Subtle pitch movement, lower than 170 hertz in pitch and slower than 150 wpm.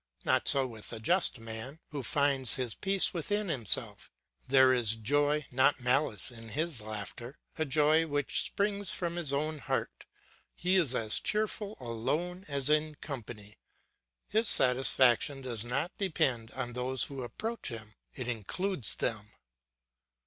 No: average, 5.0 semitones; low, 135 Hz; average, 140 wpm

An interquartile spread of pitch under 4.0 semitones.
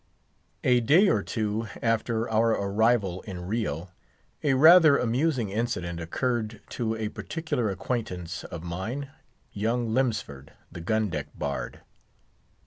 No: average, 4.8 semitones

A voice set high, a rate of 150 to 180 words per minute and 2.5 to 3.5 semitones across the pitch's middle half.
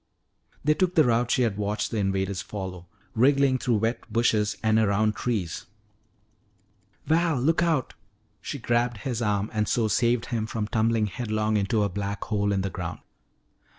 No: low, 110 Hz; average, 165 wpm; average, 3.1 semitones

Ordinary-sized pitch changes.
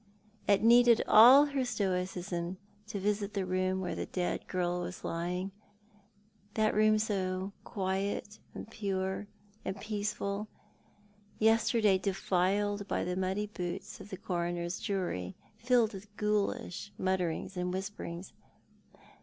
No: narrow, 2.2 semitones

